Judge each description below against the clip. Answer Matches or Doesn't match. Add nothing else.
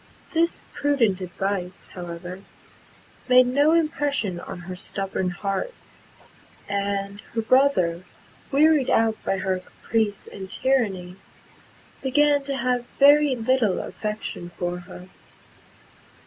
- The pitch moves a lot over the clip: Matches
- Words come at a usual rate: Doesn't match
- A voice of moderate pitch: Doesn't match